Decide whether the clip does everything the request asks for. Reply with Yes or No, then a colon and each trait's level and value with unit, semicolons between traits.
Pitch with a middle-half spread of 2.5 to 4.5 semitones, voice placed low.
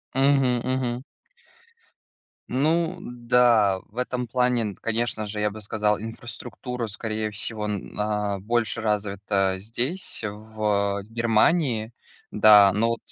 Yes: average, 2.8 semitones; low, 110 Hz